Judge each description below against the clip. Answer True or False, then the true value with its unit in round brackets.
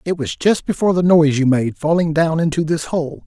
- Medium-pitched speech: True (160 Hz)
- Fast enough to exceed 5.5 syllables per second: True (5.7 syllables/s)